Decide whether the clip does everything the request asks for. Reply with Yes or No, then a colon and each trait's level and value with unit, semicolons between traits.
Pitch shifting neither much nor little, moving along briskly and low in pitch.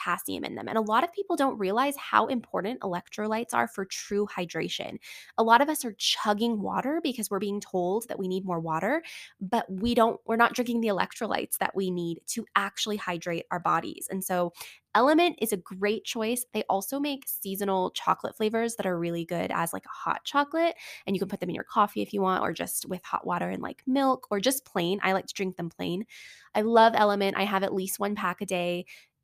No: average, 3.6 semitones; fast, 225 wpm; high, 205 Hz